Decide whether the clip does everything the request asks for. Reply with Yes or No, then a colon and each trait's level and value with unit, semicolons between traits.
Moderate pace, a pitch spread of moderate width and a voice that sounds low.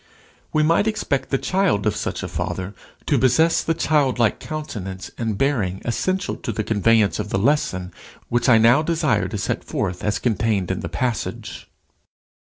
No: average, 170 wpm; wide, 7.0 semitones; low, 115 Hz